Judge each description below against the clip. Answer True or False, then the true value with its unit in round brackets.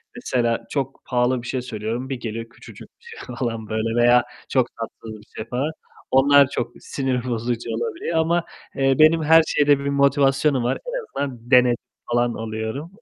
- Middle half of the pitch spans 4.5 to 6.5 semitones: False (3.2 semitones)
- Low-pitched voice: True (125 Hz)